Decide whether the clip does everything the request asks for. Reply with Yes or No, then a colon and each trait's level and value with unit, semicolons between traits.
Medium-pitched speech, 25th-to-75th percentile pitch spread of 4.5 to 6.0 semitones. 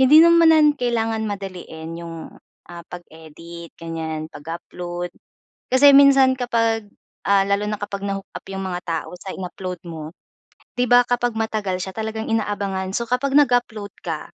No: high, 200 Hz; wide, 5.5 semitones